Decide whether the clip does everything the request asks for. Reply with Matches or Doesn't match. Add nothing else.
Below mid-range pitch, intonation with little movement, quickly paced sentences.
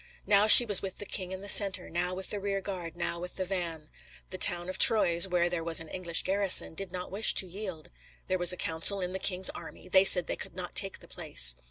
Doesn't match